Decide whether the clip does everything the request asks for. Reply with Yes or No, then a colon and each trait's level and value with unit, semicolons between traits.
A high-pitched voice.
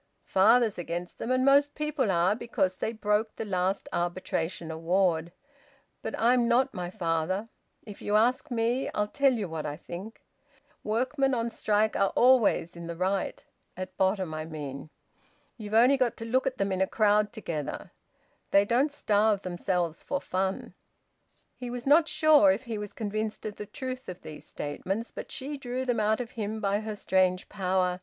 Yes: high, 210 Hz